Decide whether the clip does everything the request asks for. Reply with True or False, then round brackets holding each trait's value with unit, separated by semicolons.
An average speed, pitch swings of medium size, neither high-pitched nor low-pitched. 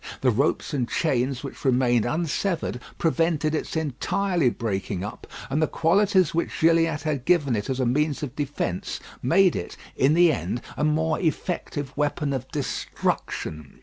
True (155 wpm; 4.4 semitones; 145 Hz)